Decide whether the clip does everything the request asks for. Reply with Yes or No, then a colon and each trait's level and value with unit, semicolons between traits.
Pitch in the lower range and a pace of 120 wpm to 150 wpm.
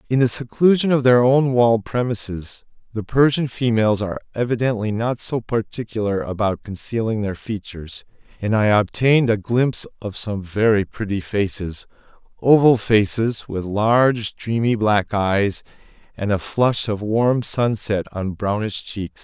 Yes: low, 110 Hz; average, 145 wpm